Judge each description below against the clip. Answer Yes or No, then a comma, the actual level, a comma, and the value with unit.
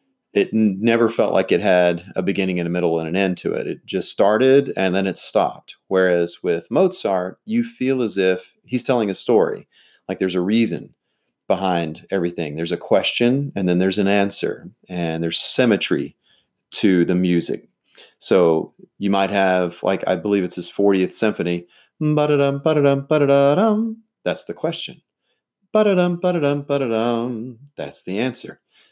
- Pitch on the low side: Yes, low, 100 Hz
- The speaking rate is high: No, average, 145 wpm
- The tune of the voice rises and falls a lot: Yes, wide, 7.6 semitones